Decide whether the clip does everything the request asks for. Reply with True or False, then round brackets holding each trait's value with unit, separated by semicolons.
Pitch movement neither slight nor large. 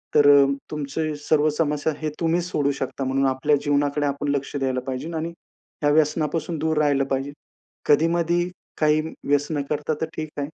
False (1.8 semitones)